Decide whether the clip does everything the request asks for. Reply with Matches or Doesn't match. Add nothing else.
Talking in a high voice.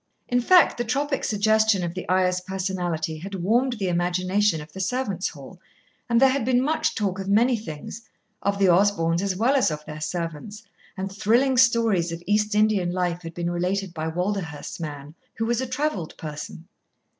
Matches